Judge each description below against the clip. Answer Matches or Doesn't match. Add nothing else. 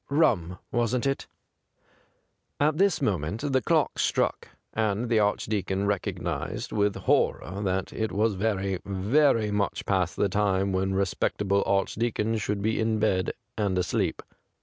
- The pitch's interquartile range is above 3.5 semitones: Doesn't match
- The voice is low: Matches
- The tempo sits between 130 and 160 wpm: Matches